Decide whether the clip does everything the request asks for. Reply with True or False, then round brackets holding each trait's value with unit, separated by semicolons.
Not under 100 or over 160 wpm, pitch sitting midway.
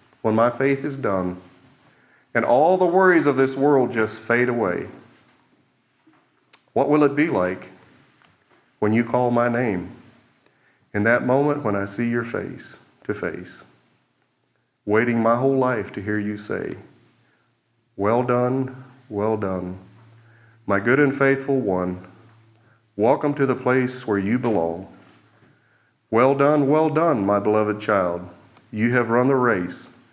False (140 wpm; 120 Hz)